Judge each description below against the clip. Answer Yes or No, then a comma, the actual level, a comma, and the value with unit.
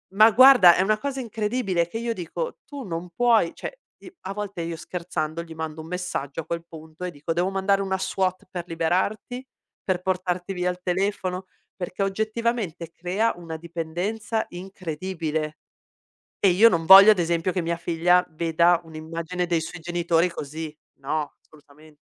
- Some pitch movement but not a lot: Yes, average, 3.1 semitones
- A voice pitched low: No, medium, 180 Hz